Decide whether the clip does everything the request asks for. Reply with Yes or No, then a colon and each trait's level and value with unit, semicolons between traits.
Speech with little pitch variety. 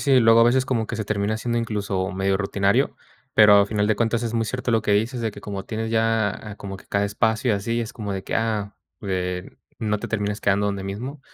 Yes: narrow, 2.1 semitones